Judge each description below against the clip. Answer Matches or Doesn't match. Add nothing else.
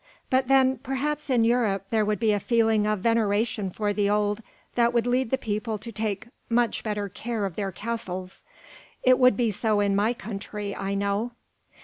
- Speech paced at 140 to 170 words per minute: Doesn't match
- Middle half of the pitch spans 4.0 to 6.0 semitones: Doesn't match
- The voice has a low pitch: Doesn't match